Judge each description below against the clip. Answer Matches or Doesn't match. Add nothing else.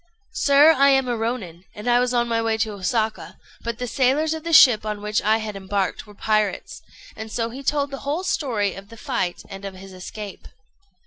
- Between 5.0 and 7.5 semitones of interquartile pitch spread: Doesn't match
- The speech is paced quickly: Matches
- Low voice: Doesn't match